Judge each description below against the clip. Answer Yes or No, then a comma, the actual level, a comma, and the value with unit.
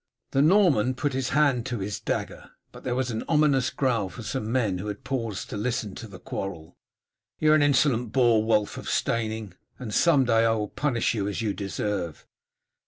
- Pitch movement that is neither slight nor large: Yes, average, 4.2 semitones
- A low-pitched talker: Yes, low, 115 Hz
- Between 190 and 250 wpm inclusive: Yes, average, 200 wpm